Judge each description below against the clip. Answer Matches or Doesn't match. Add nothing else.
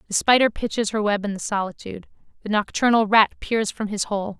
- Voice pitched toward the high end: Matches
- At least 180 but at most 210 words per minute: Matches